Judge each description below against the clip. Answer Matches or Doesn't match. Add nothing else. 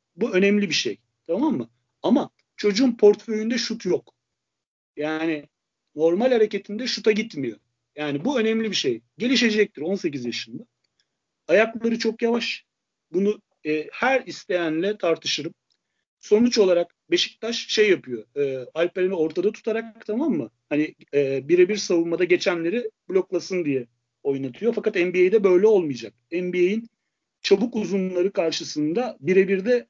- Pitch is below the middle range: Doesn't match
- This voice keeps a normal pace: Matches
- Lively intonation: Matches